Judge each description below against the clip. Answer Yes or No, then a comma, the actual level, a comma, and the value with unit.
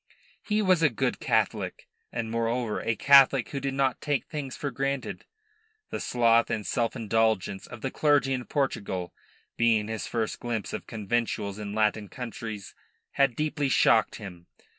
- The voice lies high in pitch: No, low, 115 Hz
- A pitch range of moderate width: Yes, average, 3.8 semitones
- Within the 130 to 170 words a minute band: Yes, average, 160 wpm